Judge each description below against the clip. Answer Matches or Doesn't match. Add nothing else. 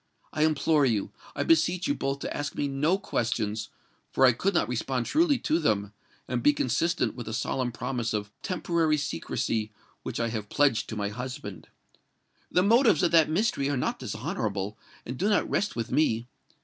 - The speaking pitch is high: Doesn't match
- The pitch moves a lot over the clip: Matches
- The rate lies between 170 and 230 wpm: Matches